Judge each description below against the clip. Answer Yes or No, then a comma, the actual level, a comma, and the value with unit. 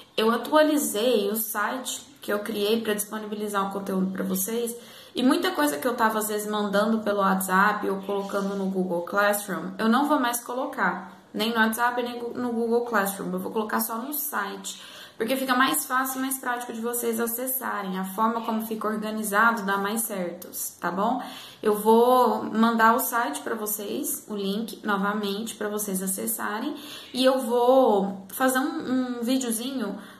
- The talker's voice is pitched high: Yes, high, 220 Hz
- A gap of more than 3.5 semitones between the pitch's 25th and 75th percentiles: No, average, 3.2 semitones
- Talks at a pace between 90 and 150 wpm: No, average, 175 wpm